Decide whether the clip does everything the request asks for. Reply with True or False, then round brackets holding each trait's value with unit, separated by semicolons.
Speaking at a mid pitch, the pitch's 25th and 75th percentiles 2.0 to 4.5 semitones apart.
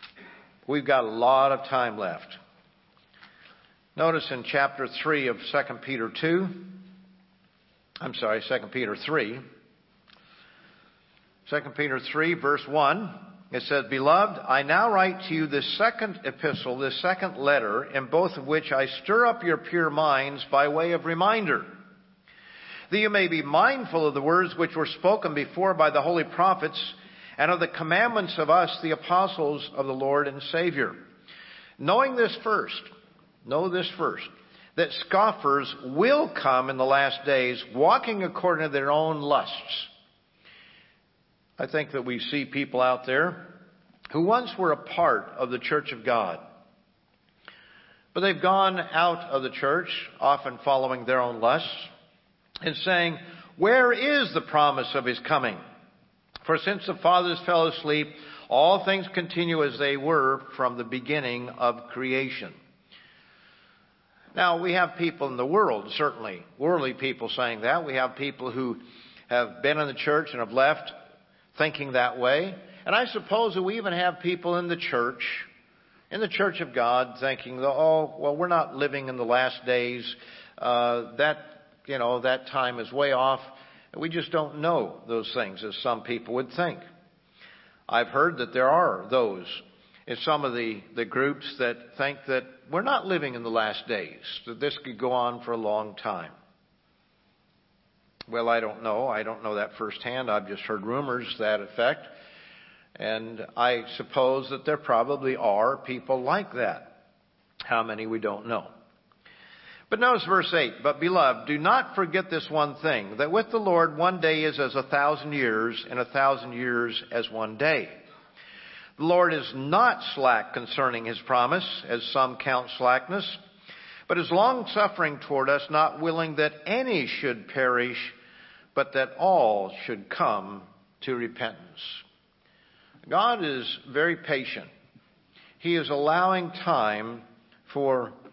False (145 Hz; 5.6 semitones)